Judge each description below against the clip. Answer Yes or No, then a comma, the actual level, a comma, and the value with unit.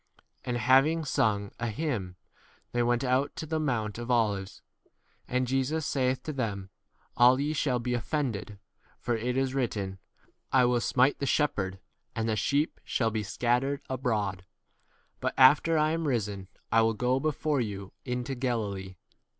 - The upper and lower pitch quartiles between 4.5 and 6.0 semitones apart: No, average, 4.0 semitones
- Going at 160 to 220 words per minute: Yes, average, 170 wpm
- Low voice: Yes, low, 125 Hz